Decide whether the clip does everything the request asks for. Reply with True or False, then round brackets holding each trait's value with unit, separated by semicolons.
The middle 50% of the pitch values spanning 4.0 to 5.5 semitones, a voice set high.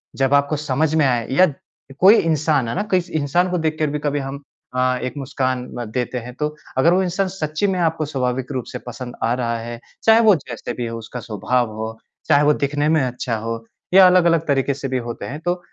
False (4.4 semitones; 140 Hz)